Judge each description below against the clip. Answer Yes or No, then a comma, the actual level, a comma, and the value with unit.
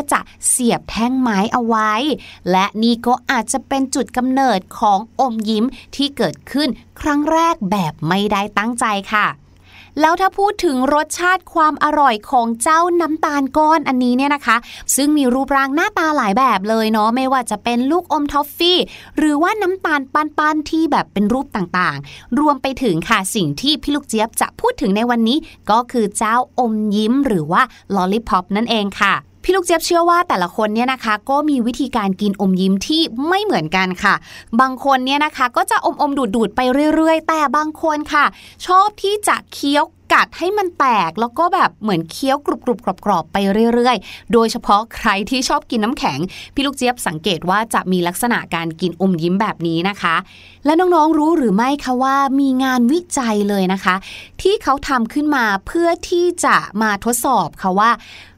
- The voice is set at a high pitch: Yes, very high, 255 Hz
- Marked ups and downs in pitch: Yes, wide, 6.0 semitones